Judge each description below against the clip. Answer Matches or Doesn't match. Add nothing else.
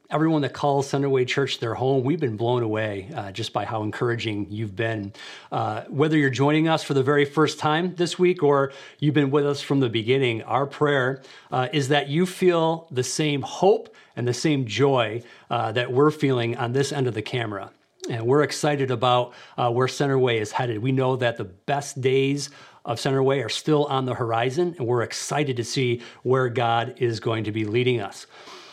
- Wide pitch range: Doesn't match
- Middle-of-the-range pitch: Doesn't match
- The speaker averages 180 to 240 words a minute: Matches